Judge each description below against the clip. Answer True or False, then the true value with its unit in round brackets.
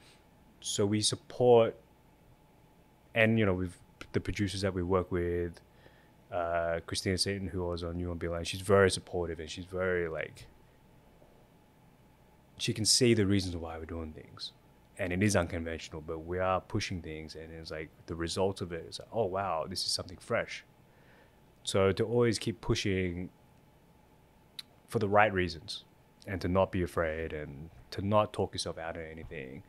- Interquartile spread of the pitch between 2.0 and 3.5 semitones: True (3.1 semitones)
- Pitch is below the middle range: True (90 Hz)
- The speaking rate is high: False (170 wpm)